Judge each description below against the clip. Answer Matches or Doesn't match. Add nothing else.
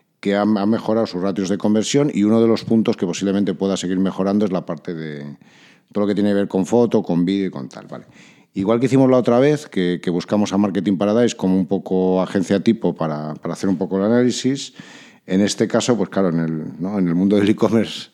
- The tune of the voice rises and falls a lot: Doesn't match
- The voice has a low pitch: Matches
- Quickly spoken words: Matches